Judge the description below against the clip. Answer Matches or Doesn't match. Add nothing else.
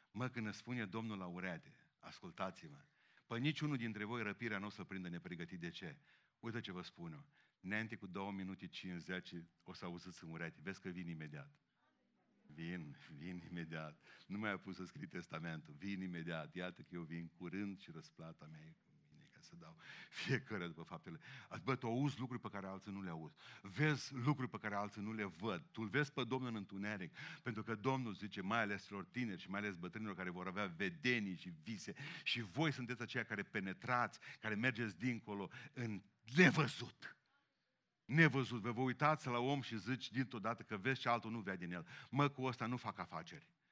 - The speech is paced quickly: Matches